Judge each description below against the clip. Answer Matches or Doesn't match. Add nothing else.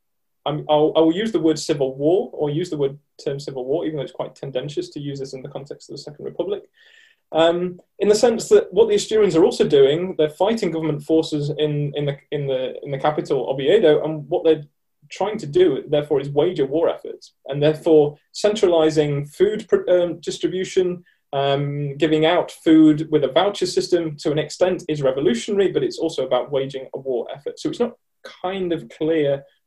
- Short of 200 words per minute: Doesn't match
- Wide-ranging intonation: Matches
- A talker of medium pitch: Matches